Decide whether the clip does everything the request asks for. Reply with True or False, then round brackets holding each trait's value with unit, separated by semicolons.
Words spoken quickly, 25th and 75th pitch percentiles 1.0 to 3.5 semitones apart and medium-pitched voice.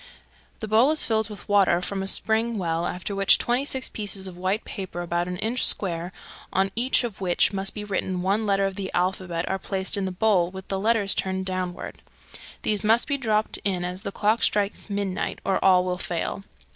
False (210 wpm; 2.6 semitones; 195 Hz)